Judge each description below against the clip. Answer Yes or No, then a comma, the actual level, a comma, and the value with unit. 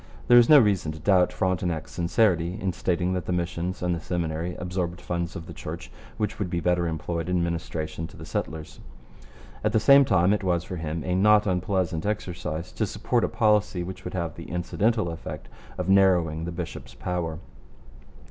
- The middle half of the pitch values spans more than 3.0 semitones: No, narrow, 2.4 semitones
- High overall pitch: No, very low, 90 Hz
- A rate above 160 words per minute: Yes, average, 190 wpm